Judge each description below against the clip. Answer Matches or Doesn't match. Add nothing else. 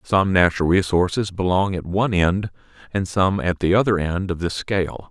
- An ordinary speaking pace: Matches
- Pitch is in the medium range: Doesn't match